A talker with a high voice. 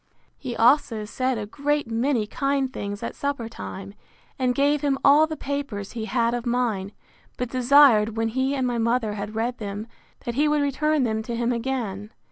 Yes: high, 245 Hz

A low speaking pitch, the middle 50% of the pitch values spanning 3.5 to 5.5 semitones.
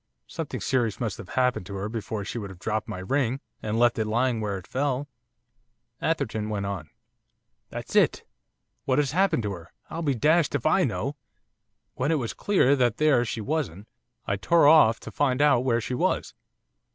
Yes: low, 120 Hz; average, 5.2 semitones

